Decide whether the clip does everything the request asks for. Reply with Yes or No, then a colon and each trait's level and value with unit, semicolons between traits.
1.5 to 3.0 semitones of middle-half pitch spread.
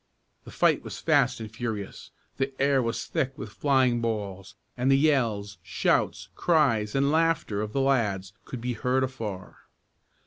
No: average, 4.6 semitones